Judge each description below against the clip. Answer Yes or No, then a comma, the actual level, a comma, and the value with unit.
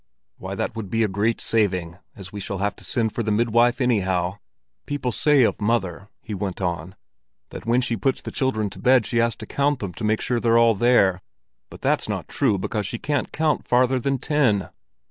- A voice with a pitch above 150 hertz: No, low, 115 Hz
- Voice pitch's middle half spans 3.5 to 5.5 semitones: Yes, average, 3.8 semitones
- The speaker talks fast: Yes, fast, 215 wpm